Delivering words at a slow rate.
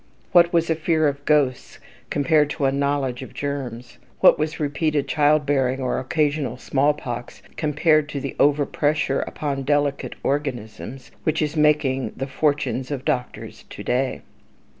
No: average, 150 wpm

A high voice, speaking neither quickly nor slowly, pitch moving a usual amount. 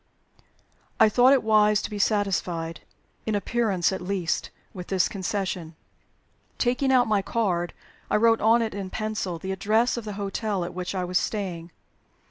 Yes: high, 200 Hz; average, 165 wpm; average, 3.2 semitones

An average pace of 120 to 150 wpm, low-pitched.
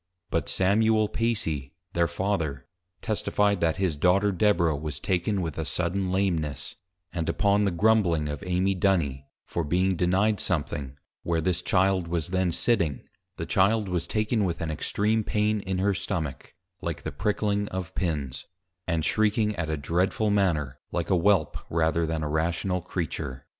No: average, 160 wpm; very low, 90 Hz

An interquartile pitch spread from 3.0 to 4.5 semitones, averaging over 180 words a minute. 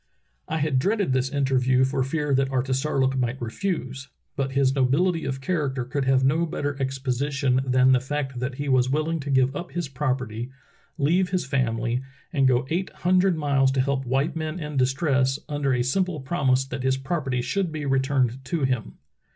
No: narrow, 2.5 semitones; average, 190 wpm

